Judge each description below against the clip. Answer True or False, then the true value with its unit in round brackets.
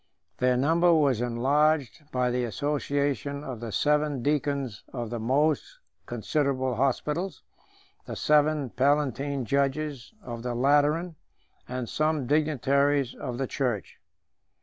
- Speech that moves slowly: True (120 wpm)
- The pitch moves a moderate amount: True (3.0 semitones)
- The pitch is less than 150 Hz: True (140 Hz)